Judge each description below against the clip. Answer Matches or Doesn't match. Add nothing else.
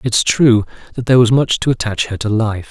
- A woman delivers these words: Doesn't match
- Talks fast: Matches